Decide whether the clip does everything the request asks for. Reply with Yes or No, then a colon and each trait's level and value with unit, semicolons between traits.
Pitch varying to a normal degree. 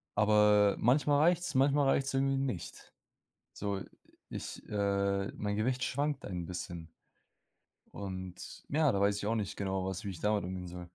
No: wide, 5.9 semitones